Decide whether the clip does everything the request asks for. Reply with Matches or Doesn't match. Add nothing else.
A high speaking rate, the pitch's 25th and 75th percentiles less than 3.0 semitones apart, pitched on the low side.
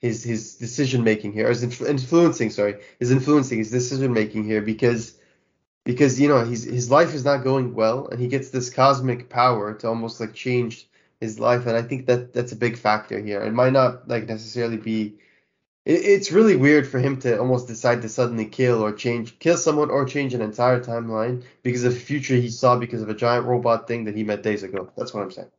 Matches